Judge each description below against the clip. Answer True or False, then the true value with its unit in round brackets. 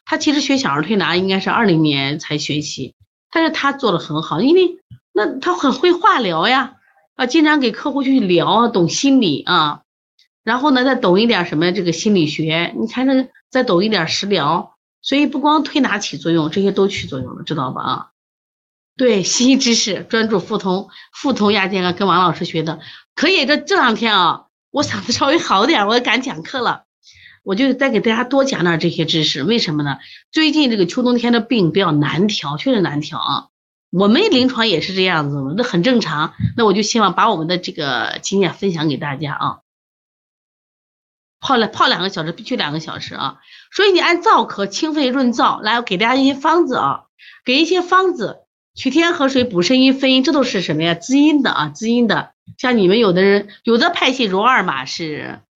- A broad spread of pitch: True (7.8 semitones)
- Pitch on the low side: False (220 Hz)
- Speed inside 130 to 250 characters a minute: False (295 characters per minute)